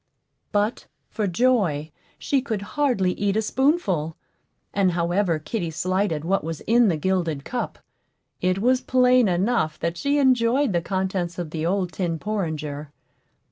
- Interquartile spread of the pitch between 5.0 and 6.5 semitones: Yes, wide, 5.6 semitones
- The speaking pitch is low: No, high, 190 Hz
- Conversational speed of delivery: Yes, average, 145 wpm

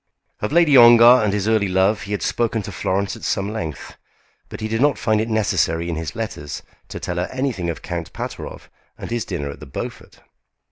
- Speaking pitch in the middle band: No, low, 105 Hz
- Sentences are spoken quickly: Yes, fast, 215 wpm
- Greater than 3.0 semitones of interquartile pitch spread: Yes, average, 4.9 semitones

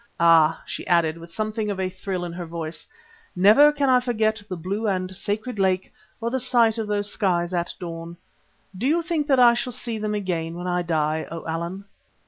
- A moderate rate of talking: No, fast, 210 wpm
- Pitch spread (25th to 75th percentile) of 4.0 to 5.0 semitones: Yes, average, 4.7 semitones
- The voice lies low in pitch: No, high, 190 Hz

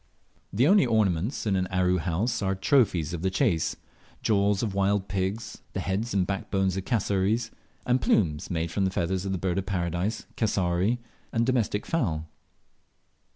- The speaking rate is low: No, average, 165 wpm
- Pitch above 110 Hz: No, very low, 95 Hz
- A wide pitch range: No, average, 3.3 semitones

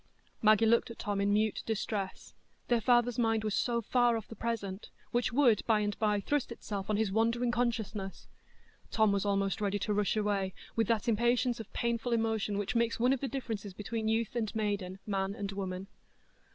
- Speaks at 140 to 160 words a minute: No, average, 190 wpm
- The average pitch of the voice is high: Yes, high, 220 Hz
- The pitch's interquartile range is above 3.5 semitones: No, narrow, 2.4 semitones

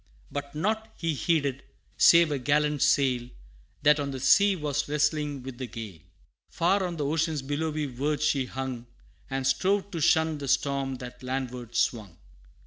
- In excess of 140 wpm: Yes, average, 160 wpm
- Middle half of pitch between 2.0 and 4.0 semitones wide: Yes, average, 3.2 semitones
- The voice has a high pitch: No, medium, 145 Hz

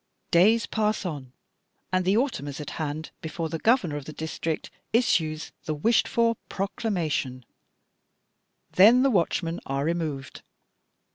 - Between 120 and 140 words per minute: Yes, slow, 135 wpm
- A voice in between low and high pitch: Yes, medium, 165 Hz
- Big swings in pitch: Yes, wide, 5.9 semitones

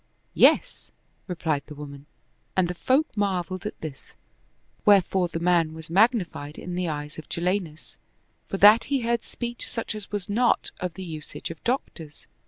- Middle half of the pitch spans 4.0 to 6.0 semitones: Yes, average, 4.5 semitones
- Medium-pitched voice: Yes, medium, 180 Hz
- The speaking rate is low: No, average, 165 wpm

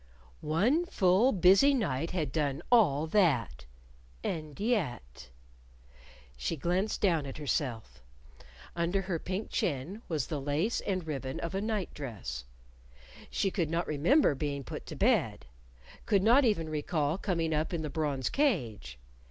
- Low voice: No, medium, 165 Hz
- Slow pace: No, average, 145 wpm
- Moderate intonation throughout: No, wide, 5.7 semitones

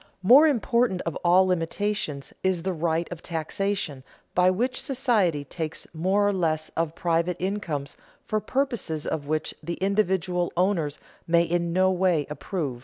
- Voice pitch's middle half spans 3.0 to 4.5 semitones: Yes, average, 3.6 semitones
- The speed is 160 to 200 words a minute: No, average, 150 wpm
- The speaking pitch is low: No, medium, 180 Hz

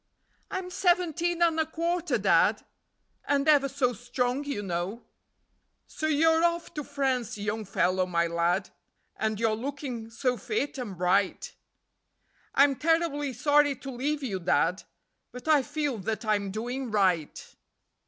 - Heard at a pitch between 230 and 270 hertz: Yes, very high, 255 Hz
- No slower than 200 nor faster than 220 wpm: No, average, 140 wpm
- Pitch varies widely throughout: Yes, wide, 6.1 semitones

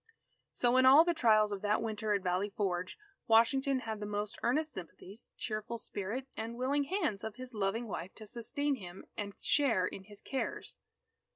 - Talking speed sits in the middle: Yes, average, 180 wpm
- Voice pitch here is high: Yes, high, 220 Hz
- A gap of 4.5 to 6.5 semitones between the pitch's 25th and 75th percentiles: No, average, 4.0 semitones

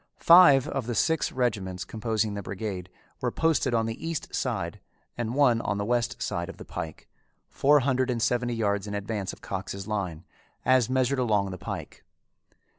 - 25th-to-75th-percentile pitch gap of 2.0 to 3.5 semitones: No, average, 4.3 semitones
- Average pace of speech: Yes, average, 180 wpm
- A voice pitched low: Yes, low, 115 Hz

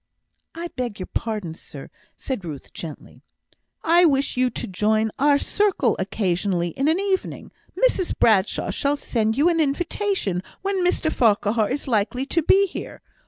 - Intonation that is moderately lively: No, wide, 8.2 semitones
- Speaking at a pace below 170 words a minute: Yes, average, 155 wpm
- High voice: Yes, very high, 255 Hz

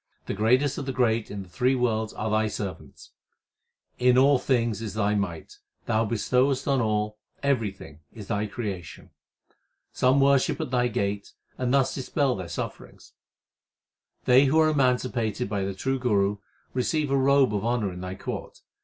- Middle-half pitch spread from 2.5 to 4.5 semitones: Yes, average, 4.2 semitones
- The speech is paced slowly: No, average, 165 wpm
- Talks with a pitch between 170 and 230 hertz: No, low, 115 Hz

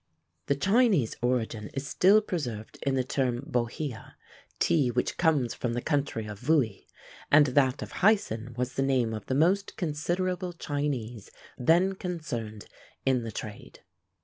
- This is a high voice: No, low, 135 Hz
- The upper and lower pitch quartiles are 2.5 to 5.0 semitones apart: No, wide, 5.4 semitones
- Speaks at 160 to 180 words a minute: No, average, 150 wpm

